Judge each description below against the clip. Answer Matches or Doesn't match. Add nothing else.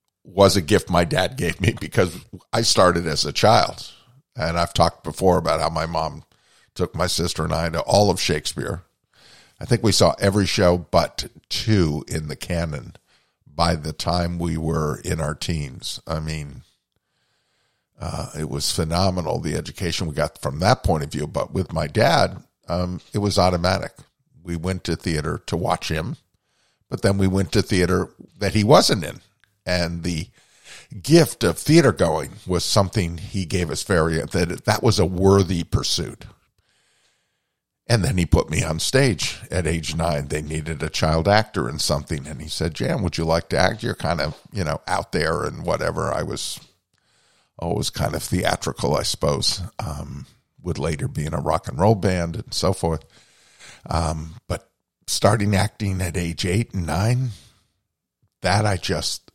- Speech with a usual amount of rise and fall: Matches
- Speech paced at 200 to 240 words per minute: Doesn't match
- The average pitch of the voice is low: Matches